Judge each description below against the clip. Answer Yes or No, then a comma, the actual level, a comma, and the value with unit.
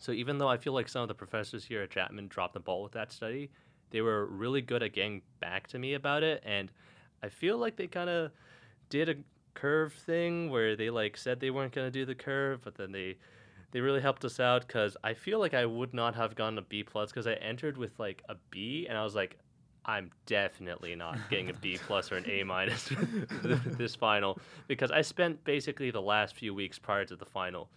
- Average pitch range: Yes, average, 4.8 semitones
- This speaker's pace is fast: Yes, fast, 235 wpm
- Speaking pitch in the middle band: No, low, 125 Hz